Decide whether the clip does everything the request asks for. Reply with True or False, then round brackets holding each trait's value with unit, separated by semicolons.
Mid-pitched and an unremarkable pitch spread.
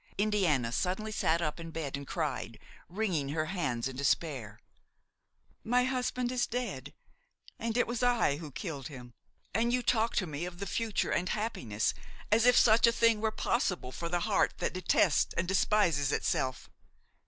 False (180 Hz; 7.8 semitones)